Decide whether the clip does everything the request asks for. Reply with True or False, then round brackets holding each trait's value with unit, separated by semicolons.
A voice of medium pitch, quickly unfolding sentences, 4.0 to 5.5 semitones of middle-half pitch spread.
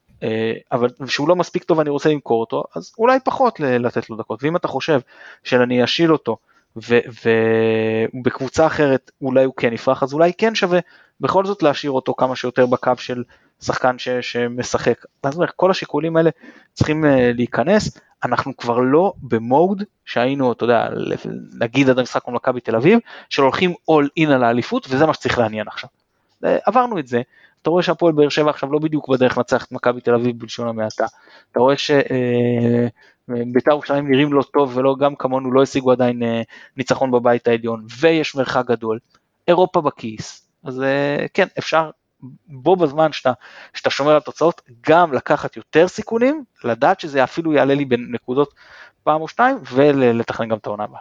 False (130 Hz; 170 wpm; 4.4 semitones)